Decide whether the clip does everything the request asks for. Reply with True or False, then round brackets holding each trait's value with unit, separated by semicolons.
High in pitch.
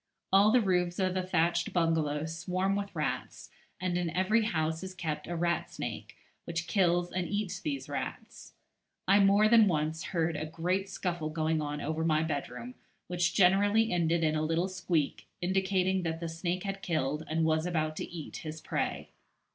False (170 Hz)